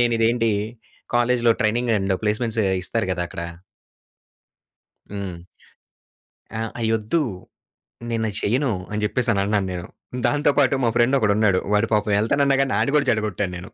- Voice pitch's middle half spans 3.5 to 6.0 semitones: No, average, 2.8 semitones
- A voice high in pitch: No, low, 110 Hz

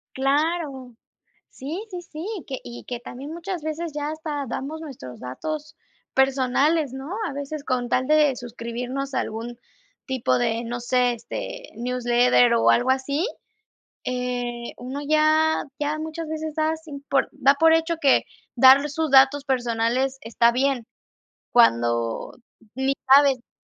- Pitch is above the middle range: Yes, very high, 270 Hz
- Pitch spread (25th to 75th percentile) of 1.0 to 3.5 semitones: No, average, 4.0 semitones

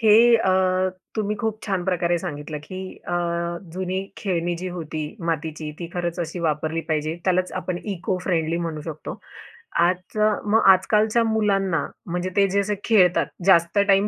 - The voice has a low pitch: No, medium, 180 Hz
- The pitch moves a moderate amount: Yes, average, 3.2 semitones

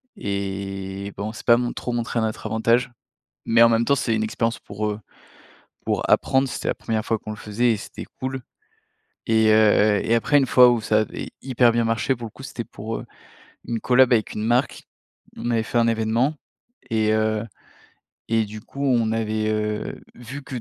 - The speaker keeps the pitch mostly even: Yes, narrow, 2.0 semitones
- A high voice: No, low, 115 Hz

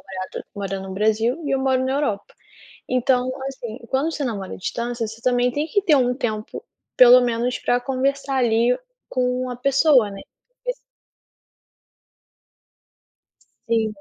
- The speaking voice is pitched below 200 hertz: No, very high, 250 Hz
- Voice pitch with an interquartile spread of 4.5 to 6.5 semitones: No, average, 2.9 semitones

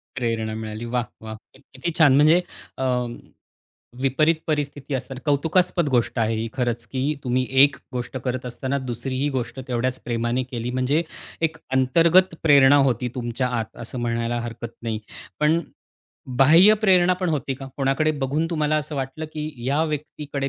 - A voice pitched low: Yes, low, 130 Hz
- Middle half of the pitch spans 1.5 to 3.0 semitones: No, average, 3.8 semitones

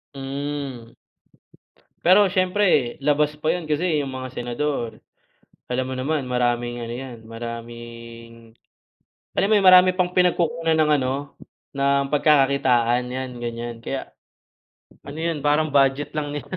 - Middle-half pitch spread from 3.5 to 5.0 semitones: Yes, average, 4.0 semitones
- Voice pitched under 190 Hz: Yes, low, 135 Hz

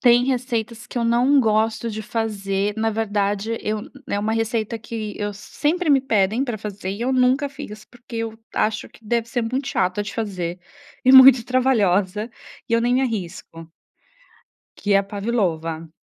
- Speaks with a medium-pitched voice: No, high, 225 Hz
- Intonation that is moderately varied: Yes, average, 3.0 semitones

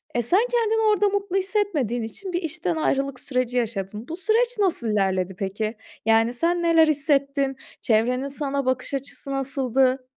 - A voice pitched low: No, very high, 275 Hz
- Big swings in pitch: Yes, wide, 6.8 semitones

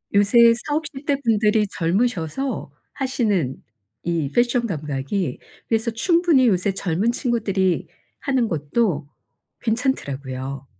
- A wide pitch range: Yes, wide, 6.8 semitones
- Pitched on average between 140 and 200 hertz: No, high, 210 Hz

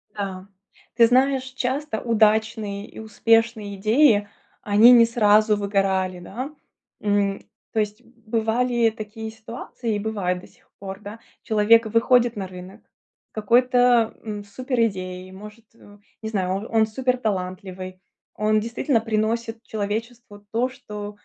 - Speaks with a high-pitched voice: Yes, high, 220 Hz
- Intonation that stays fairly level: Yes, narrow, 2.3 semitones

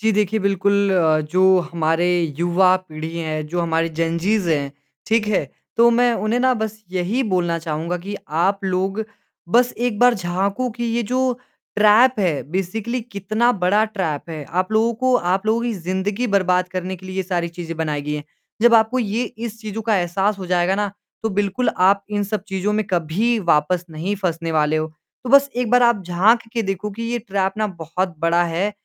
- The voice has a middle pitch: No, high, 195 Hz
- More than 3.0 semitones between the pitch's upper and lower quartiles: Yes, average, 4.1 semitones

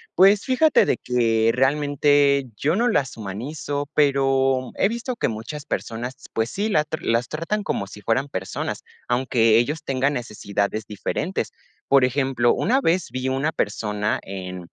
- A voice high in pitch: No, low, 135 Hz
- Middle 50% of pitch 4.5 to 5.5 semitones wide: Yes, average, 5.0 semitones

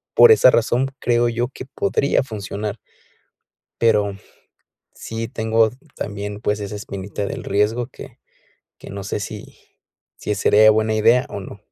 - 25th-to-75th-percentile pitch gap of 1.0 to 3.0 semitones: Yes, narrow, 2.4 semitones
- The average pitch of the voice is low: Yes, low, 110 Hz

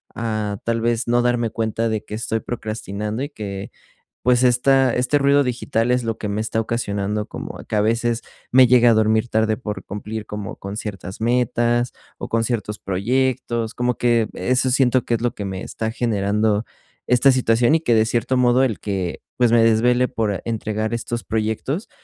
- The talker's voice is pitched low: Yes, low, 115 Hz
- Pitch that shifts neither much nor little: No, narrow, 2.3 semitones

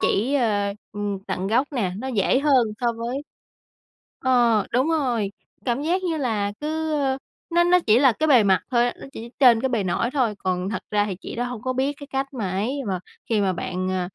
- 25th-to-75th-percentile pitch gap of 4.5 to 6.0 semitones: Yes, average, 4.9 semitones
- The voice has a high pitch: Yes, high, 240 Hz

